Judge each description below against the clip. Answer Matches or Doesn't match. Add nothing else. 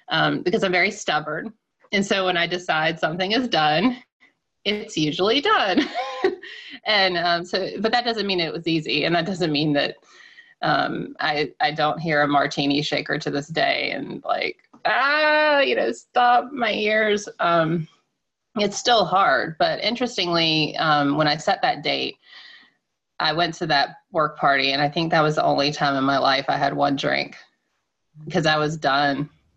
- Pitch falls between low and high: Matches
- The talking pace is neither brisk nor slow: Matches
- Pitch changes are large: Matches